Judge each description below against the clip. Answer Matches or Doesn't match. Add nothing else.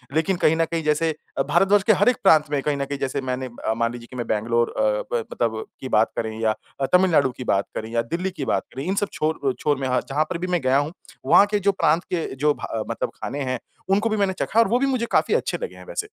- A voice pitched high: Doesn't match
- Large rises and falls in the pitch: Matches